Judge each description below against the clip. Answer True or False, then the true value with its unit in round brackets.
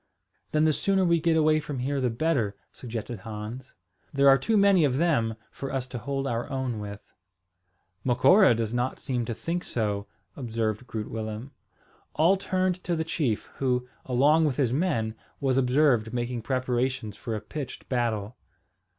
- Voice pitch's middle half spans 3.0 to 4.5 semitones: False (4.9 semitones)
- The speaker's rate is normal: True (165 wpm)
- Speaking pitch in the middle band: False (130 Hz)